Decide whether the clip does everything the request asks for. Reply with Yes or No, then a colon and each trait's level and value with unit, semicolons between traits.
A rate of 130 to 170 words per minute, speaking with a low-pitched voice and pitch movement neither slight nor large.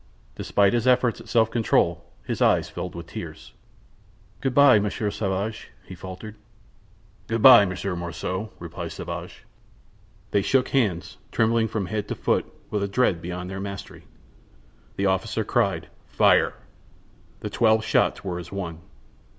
Yes: average, 145 wpm; low, 100 Hz; average, 3.7 semitones